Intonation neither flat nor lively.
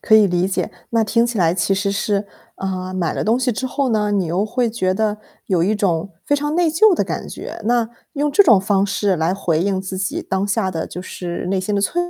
Yes: average, 3.8 semitones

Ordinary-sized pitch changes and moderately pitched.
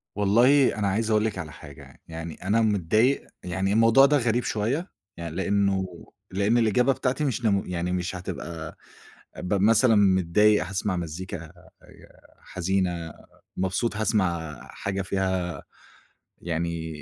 No: average, 4.0 semitones; very low, 95 Hz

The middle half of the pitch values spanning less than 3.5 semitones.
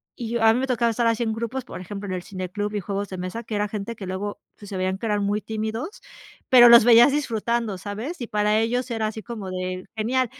Yes: average, 2.7 semitones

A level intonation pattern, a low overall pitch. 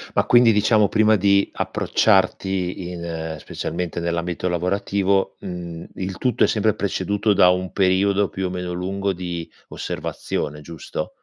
Yes: narrow, 2.3 semitones; very low, 95 Hz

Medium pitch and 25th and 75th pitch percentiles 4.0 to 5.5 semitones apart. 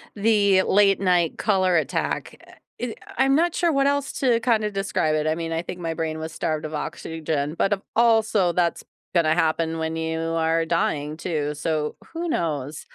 Yes: medium, 170 Hz; average, 4.5 semitones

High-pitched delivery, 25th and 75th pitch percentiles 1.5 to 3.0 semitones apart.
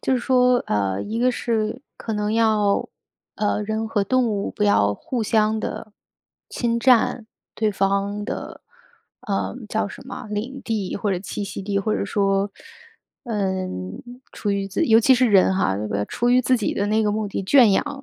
Yes: high, 210 Hz; average, 2.7 semitones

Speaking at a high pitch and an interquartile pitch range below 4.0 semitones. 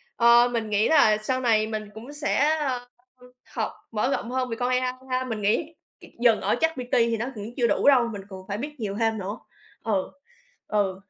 Yes: high, 235 Hz; average, 3.0 semitones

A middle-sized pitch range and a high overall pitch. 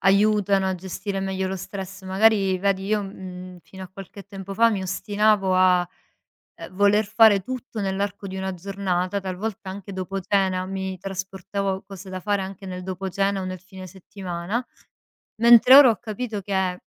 No: narrow, 1.3 semitones; high, 195 Hz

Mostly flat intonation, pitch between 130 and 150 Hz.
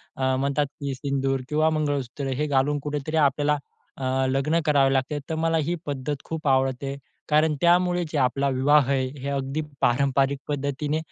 Yes: narrow, 1.9 semitones; medium, 140 Hz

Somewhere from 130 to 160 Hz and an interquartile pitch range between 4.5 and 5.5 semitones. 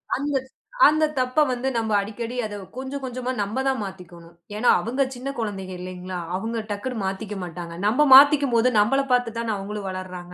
No: high, 225 Hz; average, 5.0 semitones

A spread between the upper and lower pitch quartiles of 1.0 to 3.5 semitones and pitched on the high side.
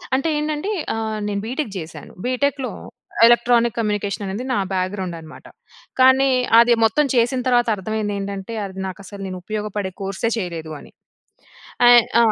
No: average, 3.9 semitones; high, 220 Hz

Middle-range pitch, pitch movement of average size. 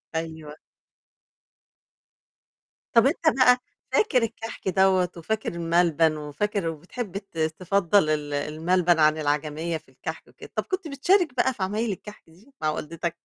No: medium, 175 Hz; wide, 5.7 semitones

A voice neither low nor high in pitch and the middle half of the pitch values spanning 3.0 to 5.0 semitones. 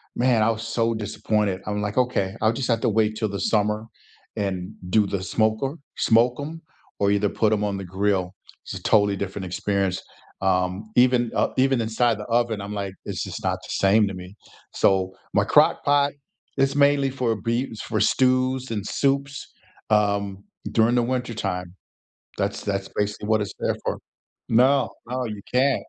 No: low, 110 Hz; average, 3.6 semitones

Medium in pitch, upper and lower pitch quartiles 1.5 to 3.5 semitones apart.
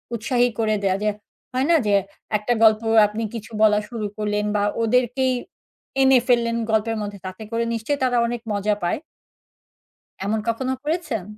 No: high, 225 Hz; average, 2.9 semitones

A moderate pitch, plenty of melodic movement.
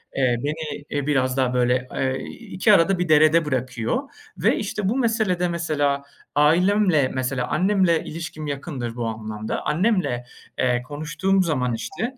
Yes: medium, 150 Hz; wide, 6.0 semitones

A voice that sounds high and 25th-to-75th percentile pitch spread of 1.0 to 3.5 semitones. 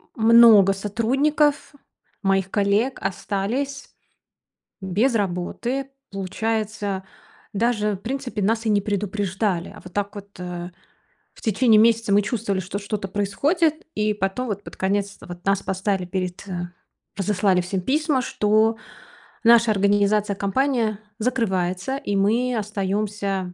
Yes: high, 205 Hz; average, 2.9 semitones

